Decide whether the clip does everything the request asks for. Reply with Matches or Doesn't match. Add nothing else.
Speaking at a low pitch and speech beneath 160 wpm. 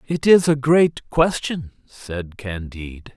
Matches